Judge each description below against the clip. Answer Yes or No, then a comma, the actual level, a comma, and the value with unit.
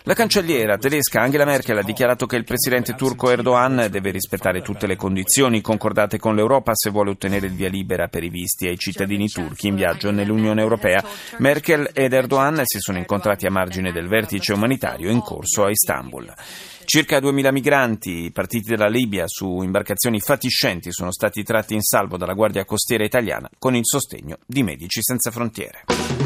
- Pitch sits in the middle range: No, low, 110 Hz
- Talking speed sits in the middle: No, fast, 175 wpm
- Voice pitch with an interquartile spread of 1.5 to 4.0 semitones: No, average, 4.5 semitones